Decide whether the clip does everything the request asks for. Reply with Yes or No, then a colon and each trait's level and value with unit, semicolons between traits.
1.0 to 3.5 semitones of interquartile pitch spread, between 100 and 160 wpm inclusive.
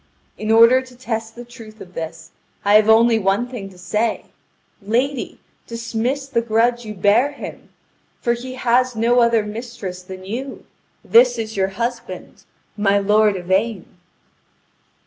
Yes: average, 3.1 semitones; average, 145 wpm